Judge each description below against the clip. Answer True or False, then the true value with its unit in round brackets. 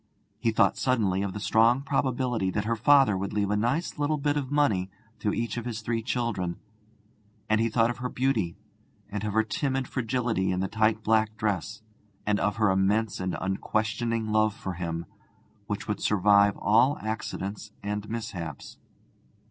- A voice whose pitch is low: True (110 Hz)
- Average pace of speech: True (170 wpm)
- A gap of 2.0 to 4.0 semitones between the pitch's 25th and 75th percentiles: True (2.9 semitones)